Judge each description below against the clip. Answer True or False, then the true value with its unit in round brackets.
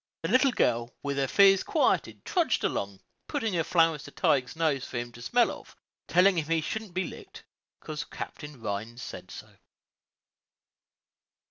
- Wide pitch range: True (7.6 semitones)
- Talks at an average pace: True (160 wpm)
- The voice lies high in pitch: False (160 Hz)